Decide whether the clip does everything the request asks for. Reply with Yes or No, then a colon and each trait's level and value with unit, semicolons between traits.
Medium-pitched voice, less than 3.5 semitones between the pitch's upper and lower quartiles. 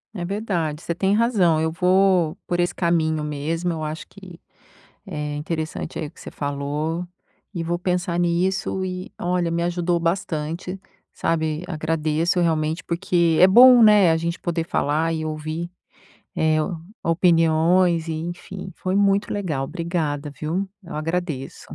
Yes: medium, 170 Hz; narrow, 2.4 semitones